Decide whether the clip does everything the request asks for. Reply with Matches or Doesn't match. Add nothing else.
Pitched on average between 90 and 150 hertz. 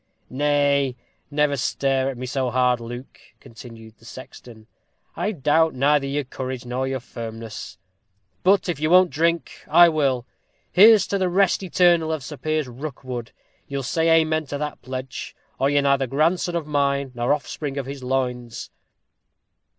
Matches